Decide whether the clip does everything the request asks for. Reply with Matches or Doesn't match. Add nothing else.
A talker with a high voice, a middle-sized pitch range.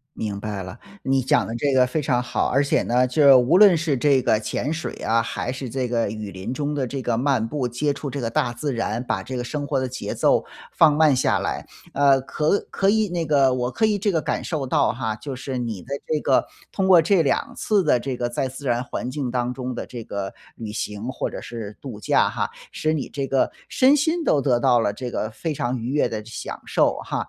Doesn't match